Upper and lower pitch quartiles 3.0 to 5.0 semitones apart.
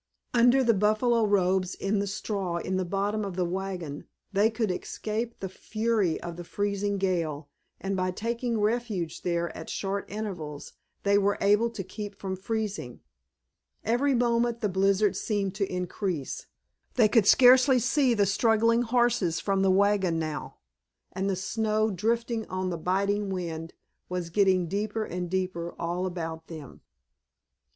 Yes: average, 3.4 semitones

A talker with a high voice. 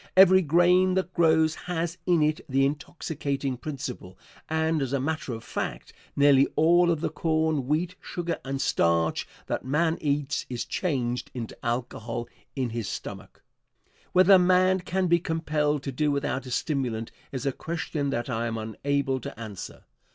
No: medium, 145 Hz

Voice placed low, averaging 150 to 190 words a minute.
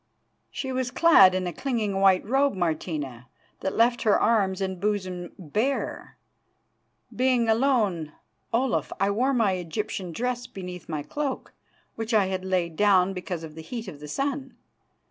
No: high, 195 Hz; average, 155 wpm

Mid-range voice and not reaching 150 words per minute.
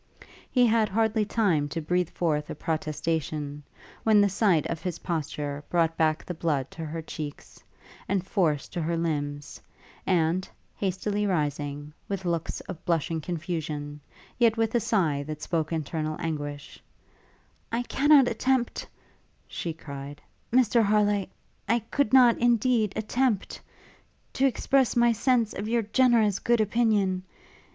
Yes: medium, 180 Hz; average, 140 wpm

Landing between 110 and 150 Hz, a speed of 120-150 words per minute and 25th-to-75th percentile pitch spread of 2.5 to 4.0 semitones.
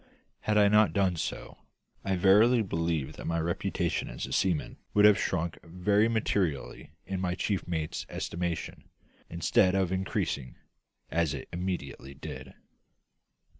No: very low, 90 Hz; slow, 135 wpm; average, 3.3 semitones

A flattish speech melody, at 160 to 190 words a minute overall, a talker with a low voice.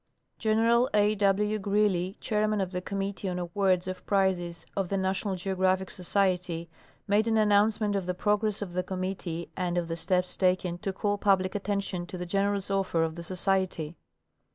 No: narrow, 2.2 semitones; average, 175 wpm; high, 190 Hz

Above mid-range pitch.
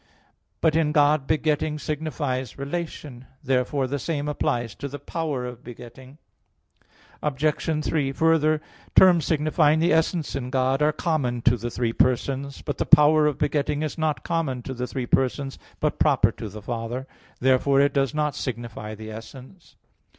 No: medium, 140 Hz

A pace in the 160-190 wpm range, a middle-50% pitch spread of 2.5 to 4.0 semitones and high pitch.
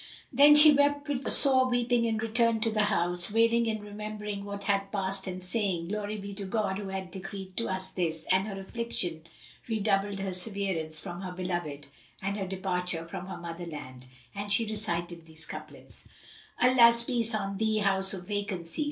Yes: average, 180 wpm; average, 3.3 semitones; high, 200 Hz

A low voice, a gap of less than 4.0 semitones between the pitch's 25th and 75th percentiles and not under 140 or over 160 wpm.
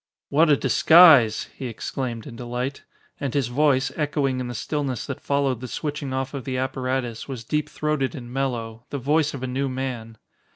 No: low, 130 Hz; narrow, 2.6 semitones; average, 190 wpm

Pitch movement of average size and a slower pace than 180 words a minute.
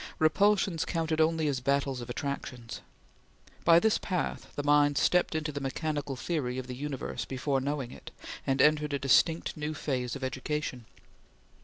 Yes: average, 3.0 semitones; average, 160 wpm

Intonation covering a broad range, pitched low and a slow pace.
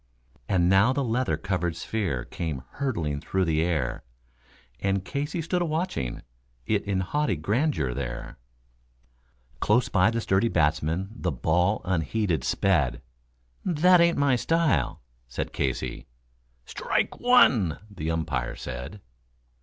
Yes: wide, 8.1 semitones; very low, 95 Hz; slow, 125 wpm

